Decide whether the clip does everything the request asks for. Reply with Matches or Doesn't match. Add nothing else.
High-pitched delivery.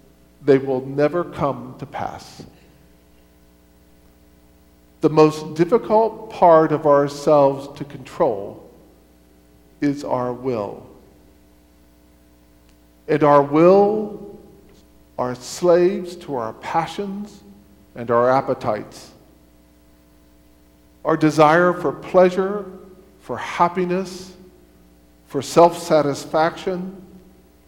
Doesn't match